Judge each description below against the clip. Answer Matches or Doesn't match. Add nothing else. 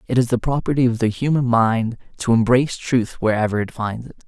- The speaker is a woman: Doesn't match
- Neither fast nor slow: Doesn't match